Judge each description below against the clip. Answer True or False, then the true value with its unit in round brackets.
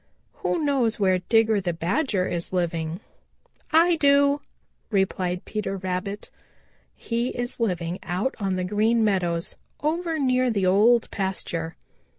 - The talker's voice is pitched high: True (205 Hz)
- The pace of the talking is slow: True (130 wpm)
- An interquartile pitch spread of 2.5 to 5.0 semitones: False (5.4 semitones)